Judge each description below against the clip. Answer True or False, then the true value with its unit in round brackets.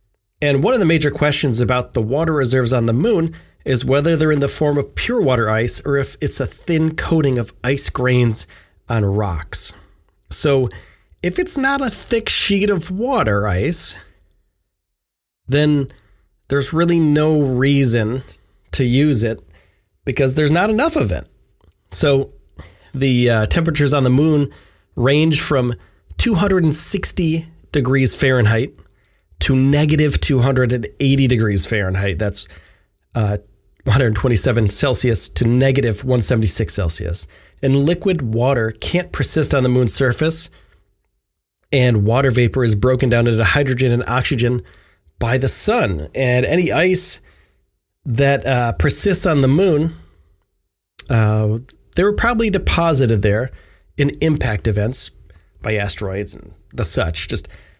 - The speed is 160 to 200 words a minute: False (135 wpm)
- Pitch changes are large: True (6.0 semitones)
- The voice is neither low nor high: False (125 Hz)